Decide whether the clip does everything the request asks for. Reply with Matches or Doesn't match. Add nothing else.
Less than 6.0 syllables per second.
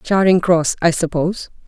Matches